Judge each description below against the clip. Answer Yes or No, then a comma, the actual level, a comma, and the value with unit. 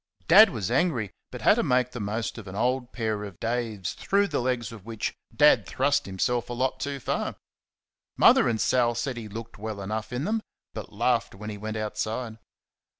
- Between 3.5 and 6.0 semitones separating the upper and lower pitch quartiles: No, average, 2.9 semitones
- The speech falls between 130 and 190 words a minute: No, average, 200 wpm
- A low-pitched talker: Yes, low, 115 Hz